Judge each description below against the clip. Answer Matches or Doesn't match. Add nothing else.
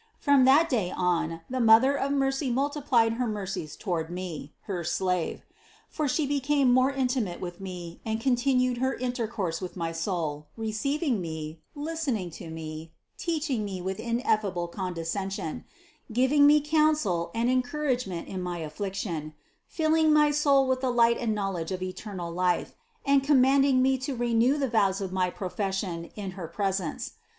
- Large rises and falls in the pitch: Matches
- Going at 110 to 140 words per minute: Doesn't match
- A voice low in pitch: Doesn't match